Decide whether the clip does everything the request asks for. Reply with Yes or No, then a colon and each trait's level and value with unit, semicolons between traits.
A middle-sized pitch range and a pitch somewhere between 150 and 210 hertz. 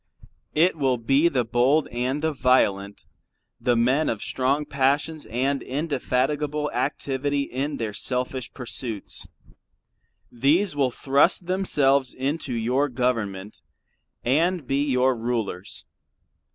No: average, 3.0 semitones; low, 135 Hz